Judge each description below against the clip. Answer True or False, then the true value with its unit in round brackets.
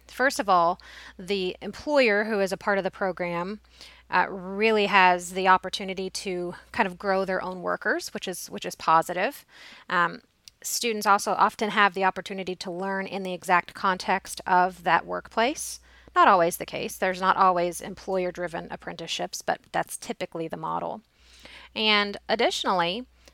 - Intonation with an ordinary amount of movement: False (2.0 semitones)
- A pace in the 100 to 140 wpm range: False (160 wpm)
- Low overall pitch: False (190 Hz)